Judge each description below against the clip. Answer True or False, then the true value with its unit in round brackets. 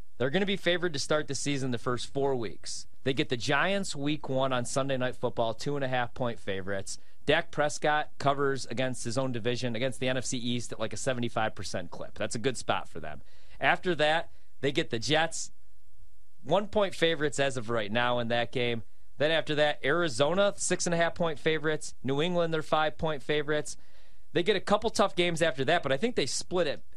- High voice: False (135 Hz)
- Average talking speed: False (215 wpm)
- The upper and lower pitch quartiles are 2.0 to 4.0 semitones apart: False (4.8 semitones)